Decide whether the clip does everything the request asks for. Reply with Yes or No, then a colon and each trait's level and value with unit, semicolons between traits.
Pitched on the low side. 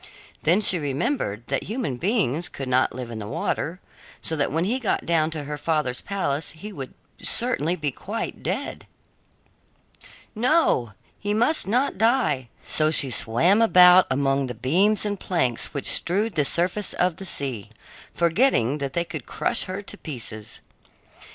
No: medium, 165 Hz